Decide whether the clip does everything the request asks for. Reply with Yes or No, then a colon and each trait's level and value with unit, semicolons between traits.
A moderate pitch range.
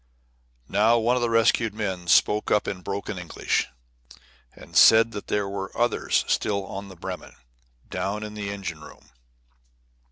No: narrow, 2.3 semitones